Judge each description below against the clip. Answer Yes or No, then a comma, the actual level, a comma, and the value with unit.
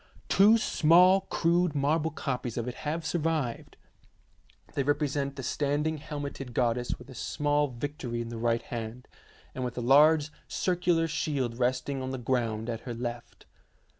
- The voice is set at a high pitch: No, medium, 140 Hz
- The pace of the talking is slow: No, average, 155 wpm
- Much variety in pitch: No, average, 4.2 semitones